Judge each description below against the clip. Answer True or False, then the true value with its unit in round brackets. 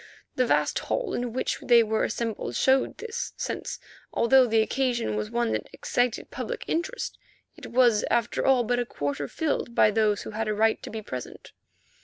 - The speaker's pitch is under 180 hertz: False (235 Hz)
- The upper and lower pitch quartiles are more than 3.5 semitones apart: False (3.2 semitones)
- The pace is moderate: True (185 wpm)